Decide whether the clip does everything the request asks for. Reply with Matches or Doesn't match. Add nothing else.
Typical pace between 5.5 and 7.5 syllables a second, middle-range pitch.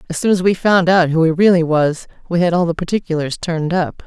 Matches